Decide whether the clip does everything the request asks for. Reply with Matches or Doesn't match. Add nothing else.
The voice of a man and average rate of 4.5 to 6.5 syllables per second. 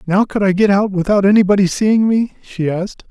Matches